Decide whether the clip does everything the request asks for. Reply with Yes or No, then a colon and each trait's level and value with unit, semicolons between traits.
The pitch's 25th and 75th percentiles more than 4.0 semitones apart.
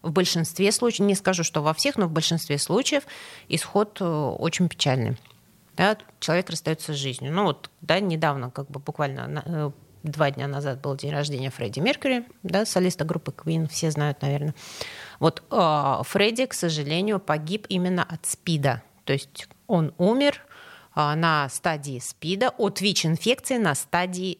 Yes: average, 5.2 semitones